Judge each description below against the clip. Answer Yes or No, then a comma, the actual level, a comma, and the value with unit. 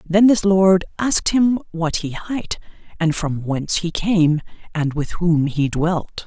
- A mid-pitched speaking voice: Yes, medium, 175 Hz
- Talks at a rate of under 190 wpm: Yes, average, 170 wpm